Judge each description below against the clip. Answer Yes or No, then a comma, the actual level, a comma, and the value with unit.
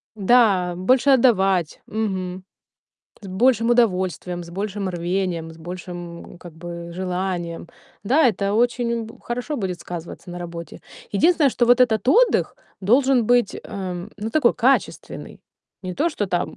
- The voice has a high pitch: Yes, high, 195 Hz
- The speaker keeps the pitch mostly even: No, average, 5.2 semitones